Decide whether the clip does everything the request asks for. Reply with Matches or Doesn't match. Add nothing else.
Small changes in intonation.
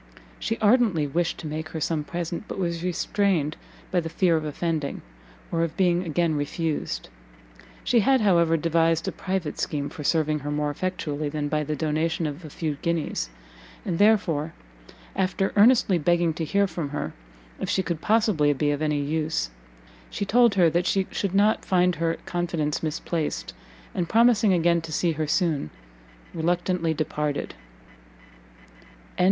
Doesn't match